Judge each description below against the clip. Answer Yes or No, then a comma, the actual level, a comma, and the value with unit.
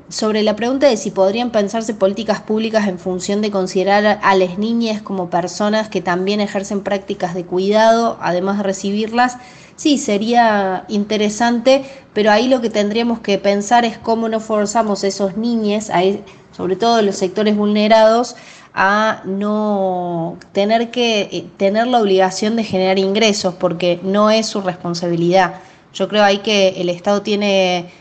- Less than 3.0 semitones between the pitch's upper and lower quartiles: Yes, narrow, 2.6 semitones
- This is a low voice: No, high, 205 Hz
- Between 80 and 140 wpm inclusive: No, average, 150 wpm